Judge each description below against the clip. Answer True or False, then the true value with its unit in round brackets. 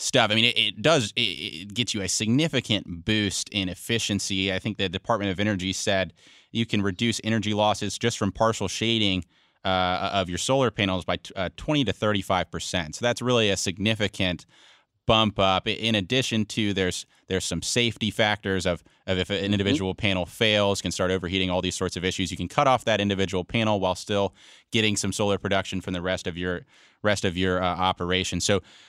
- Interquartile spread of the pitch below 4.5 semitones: True (2.8 semitones)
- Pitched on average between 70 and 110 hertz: True (100 Hz)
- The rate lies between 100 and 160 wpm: False (200 wpm)